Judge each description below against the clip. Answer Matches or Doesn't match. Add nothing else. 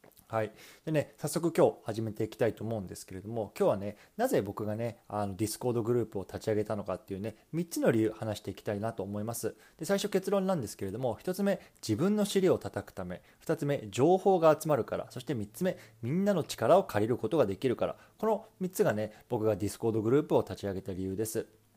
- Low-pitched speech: Matches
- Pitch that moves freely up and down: Matches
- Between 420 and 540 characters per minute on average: Matches